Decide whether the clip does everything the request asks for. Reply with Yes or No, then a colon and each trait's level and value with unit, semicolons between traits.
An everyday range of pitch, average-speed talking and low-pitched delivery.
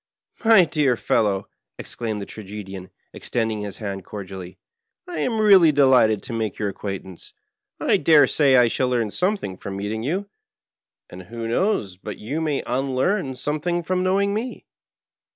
No: wide, 8.9 semitones; average, 160 wpm; low, 120 Hz